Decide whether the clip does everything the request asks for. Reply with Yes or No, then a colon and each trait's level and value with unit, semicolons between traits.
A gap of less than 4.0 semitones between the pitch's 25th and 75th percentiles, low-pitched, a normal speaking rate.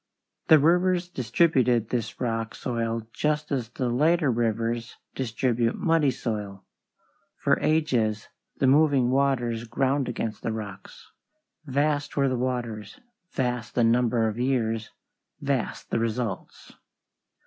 No: average, 3.4 semitones; low, 125 Hz; slow, 120 wpm